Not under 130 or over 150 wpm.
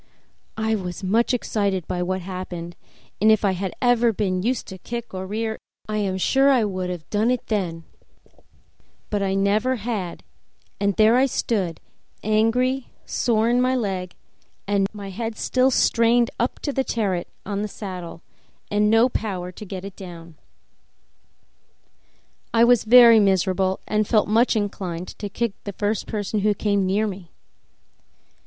No: average, 160 wpm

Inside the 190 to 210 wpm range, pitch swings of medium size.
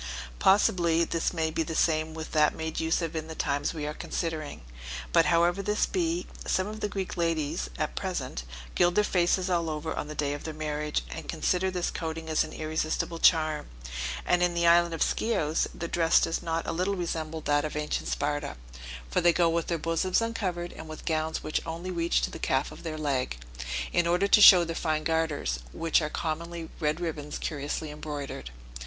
No: average, 200 wpm; narrow, 2.0 semitones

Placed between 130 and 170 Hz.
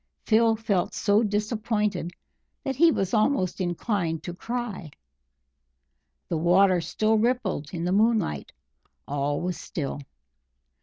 No: high, 200 Hz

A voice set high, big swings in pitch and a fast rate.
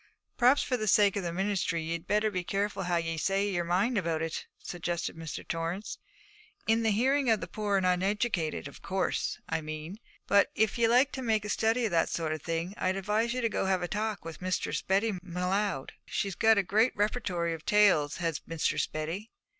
No: high, 195 Hz; average, 4.2 semitones; fast, 210 wpm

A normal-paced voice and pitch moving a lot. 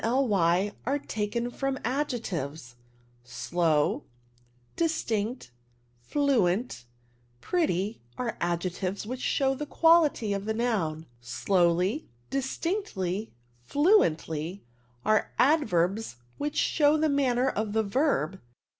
No: slow, 95 wpm; wide, 7.6 semitones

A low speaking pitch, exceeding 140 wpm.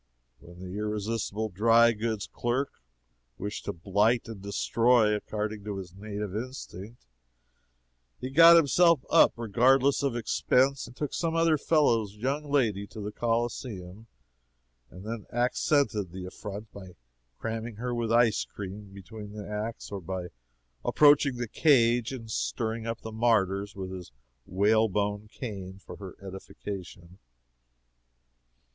No: low, 110 Hz; slow, 135 wpm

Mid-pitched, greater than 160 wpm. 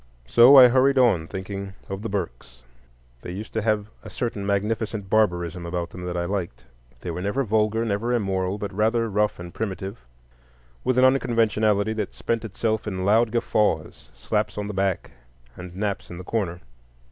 No: low, 105 Hz; average, 175 wpm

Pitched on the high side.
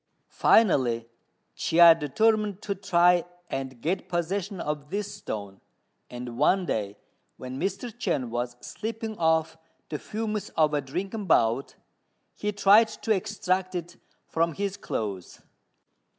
No: medium, 175 Hz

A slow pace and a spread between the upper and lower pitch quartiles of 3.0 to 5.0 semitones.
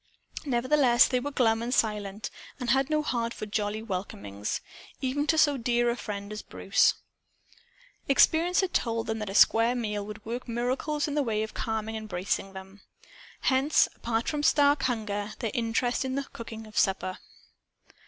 No: average, 170 wpm; average, 3.6 semitones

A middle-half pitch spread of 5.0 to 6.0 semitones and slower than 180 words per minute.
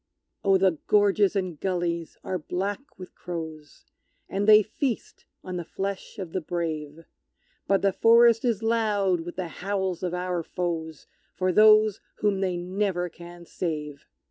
No: average, 2.9 semitones; average, 150 wpm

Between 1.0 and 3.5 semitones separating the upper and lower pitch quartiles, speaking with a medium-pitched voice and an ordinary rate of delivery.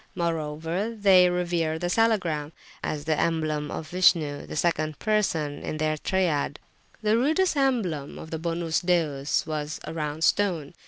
Yes: average, 3.2 semitones; medium, 165 Hz; average, 150 wpm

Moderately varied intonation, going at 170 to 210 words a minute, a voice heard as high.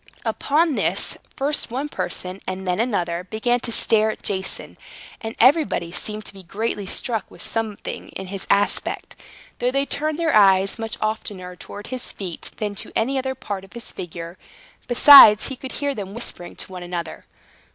Yes: average, 5.0 semitones; average, 175 wpm; high, 215 Hz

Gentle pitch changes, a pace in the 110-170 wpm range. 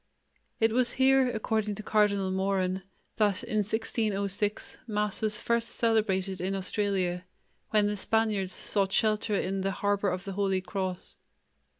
Yes: narrow, 2.2 semitones; average, 140 wpm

